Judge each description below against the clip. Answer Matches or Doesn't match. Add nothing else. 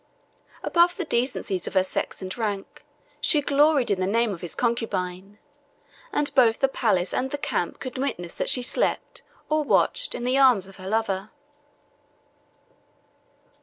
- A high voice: Matches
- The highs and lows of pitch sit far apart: Matches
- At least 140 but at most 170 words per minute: Matches